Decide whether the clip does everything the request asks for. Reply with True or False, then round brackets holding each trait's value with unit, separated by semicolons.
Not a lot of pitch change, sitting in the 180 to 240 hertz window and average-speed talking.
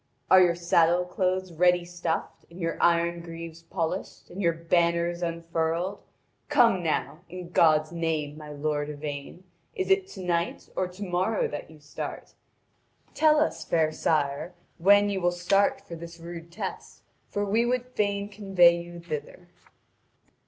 False (2.2 semitones; 170 Hz; 150 wpm)